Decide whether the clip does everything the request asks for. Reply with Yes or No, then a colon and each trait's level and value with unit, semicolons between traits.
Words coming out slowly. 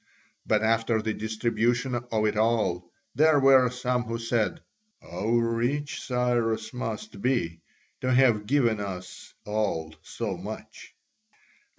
Yes: slow, 120 wpm